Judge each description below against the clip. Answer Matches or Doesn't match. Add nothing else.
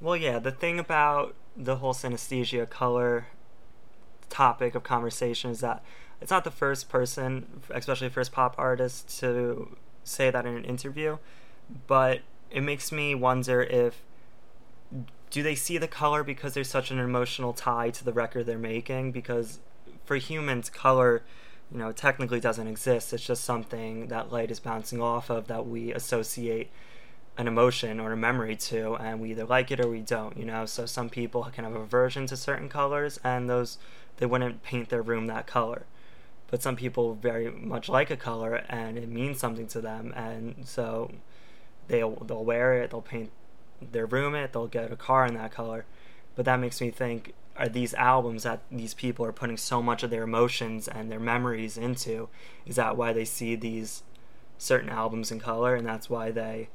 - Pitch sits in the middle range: Doesn't match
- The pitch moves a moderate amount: Doesn't match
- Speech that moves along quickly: Doesn't match